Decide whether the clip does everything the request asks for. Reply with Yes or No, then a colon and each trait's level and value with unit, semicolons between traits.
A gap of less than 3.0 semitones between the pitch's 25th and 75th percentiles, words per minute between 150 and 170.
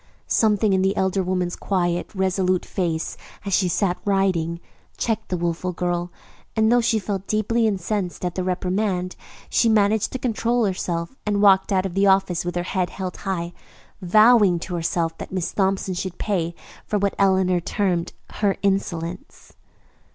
Yes: narrow, 2.4 semitones; average, 165 wpm